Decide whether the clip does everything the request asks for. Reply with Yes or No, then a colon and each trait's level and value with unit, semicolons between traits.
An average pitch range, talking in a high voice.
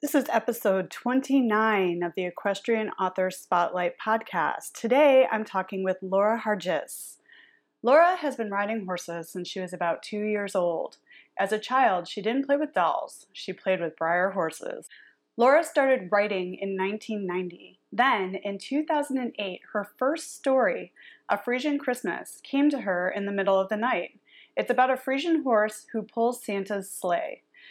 No: wide, 5.7 semitones; high, 215 Hz